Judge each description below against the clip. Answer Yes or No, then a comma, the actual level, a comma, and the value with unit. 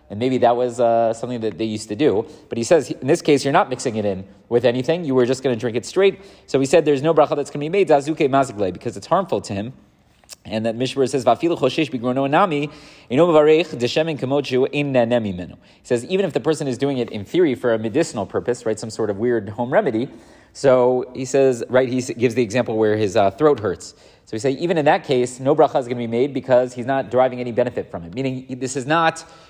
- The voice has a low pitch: Yes, low, 130 Hz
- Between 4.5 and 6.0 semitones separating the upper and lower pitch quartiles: No, average, 3.6 semitones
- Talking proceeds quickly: Yes, fast, 230 wpm